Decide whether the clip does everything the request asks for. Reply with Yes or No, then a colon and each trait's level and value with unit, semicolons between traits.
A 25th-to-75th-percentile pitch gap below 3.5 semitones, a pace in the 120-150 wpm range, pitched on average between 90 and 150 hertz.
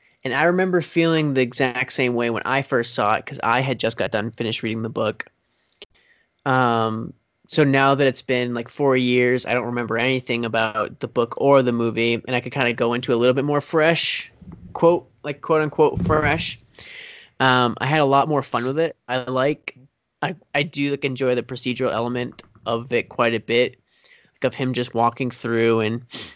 No: average, 2.8 semitones; fast, 205 wpm; low, 125 Hz